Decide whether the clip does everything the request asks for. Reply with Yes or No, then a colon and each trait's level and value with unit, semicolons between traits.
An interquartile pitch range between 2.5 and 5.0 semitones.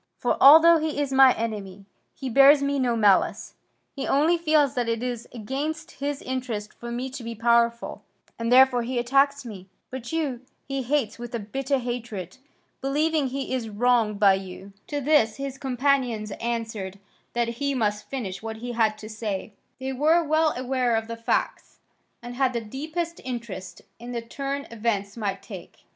Yes: average, 3.7 semitones